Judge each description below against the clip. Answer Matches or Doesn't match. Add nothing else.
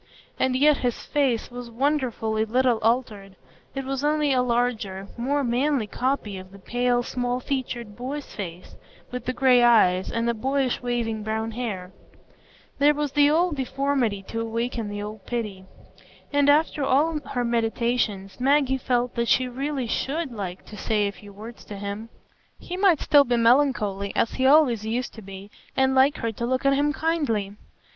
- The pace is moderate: Matches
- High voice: Matches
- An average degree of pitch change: Matches